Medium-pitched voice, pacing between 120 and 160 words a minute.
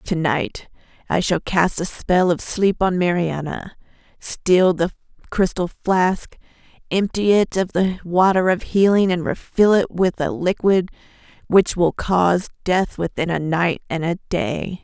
Yes: medium, 180 Hz; average, 155 wpm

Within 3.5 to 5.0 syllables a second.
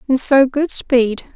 Yes: 3.6 syllables/s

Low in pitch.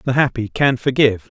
Yes: low, 125 Hz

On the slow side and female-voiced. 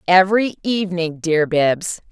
Yes: slow, 115 wpm; female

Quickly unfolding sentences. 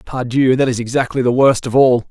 Yes: fast, 230 wpm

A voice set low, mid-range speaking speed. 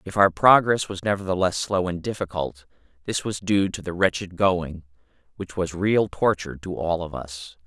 Yes: very low, 90 Hz; average, 180 wpm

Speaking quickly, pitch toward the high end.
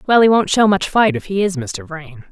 Yes: fast, 285 wpm; high, 200 Hz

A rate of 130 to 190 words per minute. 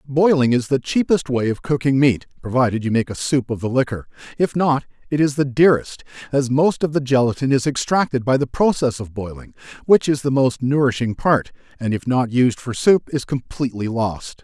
No: fast, 205 wpm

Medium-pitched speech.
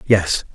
No: low, 100 Hz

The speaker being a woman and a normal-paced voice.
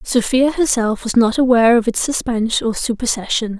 Yes: female; average, 165 wpm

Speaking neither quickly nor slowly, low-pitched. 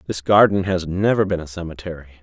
Yes: average, 190 wpm; very low, 90 Hz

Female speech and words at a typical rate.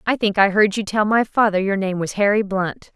No: female; fast, 265 wpm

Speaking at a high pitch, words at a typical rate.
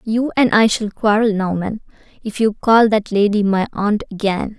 Yes: high, 210 Hz; average, 185 wpm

